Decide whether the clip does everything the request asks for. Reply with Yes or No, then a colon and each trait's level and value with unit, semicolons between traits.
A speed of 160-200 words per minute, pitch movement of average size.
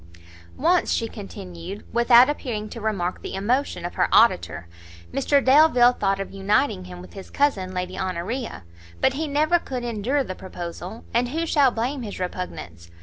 No: average, 165 wpm; wide, 6.1 semitones